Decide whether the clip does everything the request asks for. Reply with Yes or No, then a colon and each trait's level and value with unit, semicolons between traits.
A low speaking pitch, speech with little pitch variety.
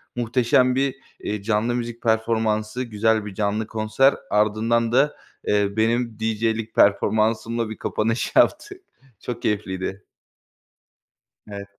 Yes: low, 110 Hz; narrow, 1.8 semitones